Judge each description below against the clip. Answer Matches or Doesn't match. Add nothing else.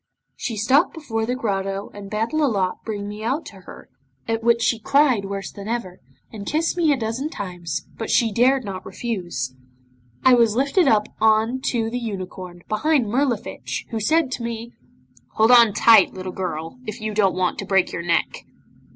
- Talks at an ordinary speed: Matches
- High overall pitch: Matches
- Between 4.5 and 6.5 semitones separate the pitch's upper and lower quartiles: Doesn't match